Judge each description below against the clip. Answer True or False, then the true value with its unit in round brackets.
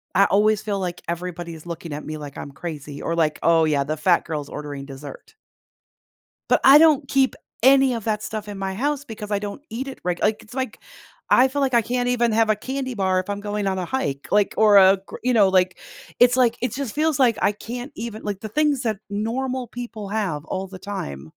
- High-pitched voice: True (210 Hz)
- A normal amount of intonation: False (5.9 semitones)